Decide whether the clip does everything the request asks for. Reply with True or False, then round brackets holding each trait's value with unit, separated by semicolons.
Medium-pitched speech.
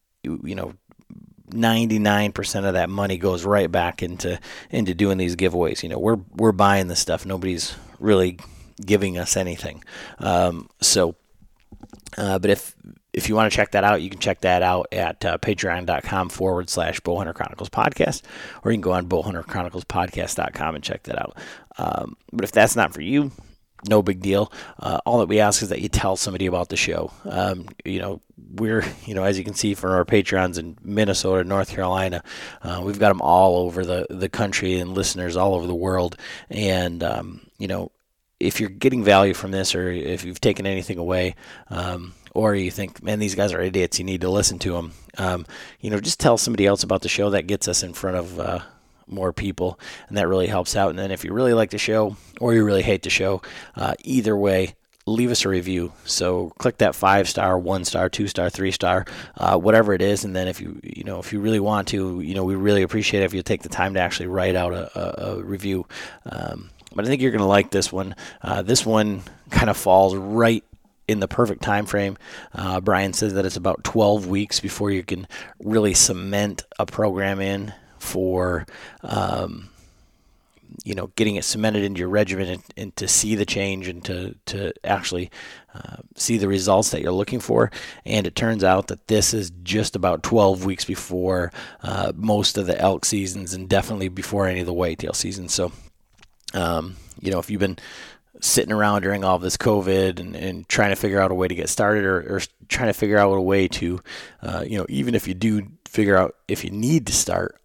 False (95 Hz)